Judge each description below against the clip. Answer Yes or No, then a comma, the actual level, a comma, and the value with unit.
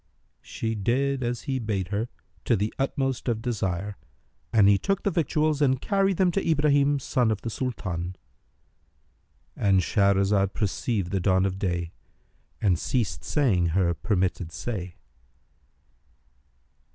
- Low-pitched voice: Yes, low, 105 Hz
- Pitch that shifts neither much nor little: No, wide, 5.9 semitones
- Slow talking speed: Yes, slow, 130 wpm